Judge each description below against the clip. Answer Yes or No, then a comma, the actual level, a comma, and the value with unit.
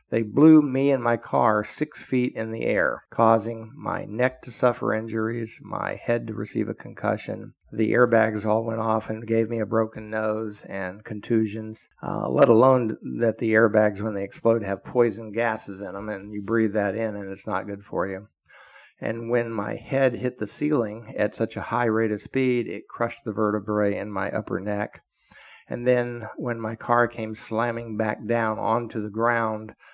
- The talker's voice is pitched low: Yes, low, 110 Hz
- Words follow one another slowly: No, average, 190 wpm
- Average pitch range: No, narrow, 1.7 semitones